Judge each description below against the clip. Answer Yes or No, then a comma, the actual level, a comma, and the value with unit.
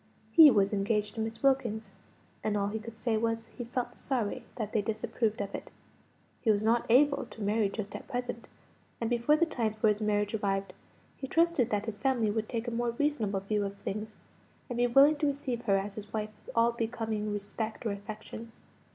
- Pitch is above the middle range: Yes, high, 225 Hz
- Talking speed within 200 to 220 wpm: Yes, fast, 205 wpm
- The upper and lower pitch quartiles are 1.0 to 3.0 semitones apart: Yes, narrow, 2.5 semitones